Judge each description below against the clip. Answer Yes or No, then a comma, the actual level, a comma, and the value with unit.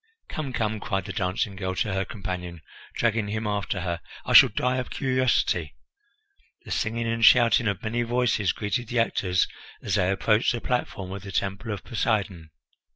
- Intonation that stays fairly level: No, average, 3.6 semitones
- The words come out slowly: No, average, 175 wpm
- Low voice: Yes, low, 105 Hz